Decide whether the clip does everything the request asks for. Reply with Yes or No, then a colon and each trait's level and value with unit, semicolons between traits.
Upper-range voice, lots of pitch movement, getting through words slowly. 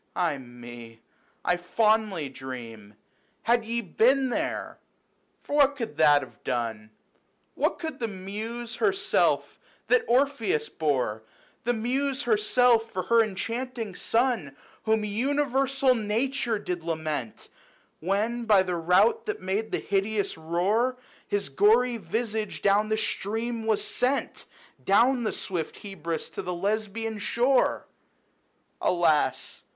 Yes: high, 215 Hz; wide, 5.8 semitones; slow, 130 wpm